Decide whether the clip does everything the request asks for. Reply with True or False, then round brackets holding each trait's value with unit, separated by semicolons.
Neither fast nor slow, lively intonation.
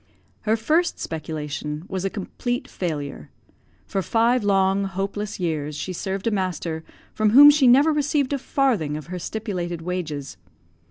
True (150 wpm; 6.2 semitones)